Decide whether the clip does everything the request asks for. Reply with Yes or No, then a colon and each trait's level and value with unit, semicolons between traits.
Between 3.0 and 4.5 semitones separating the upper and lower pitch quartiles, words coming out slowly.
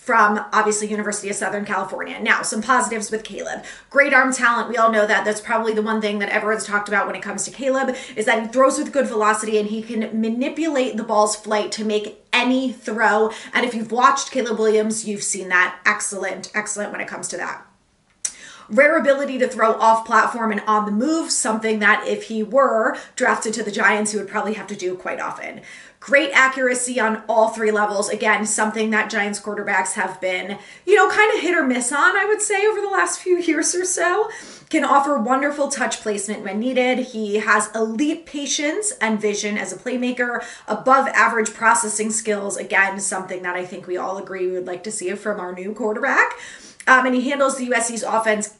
No: average, 3.7 semitones; fast, 205 wpm